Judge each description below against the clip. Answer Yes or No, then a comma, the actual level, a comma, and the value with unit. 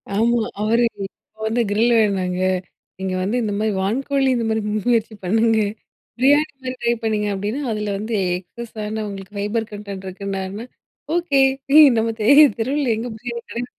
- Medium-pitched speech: No, high, 220 Hz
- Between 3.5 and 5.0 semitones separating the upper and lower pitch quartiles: No, average, 2.7 semitones